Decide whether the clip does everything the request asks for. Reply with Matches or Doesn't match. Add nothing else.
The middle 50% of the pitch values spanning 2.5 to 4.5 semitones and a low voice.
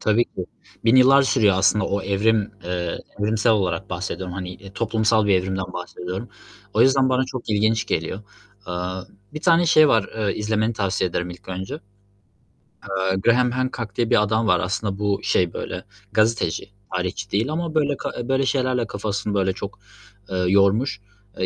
Matches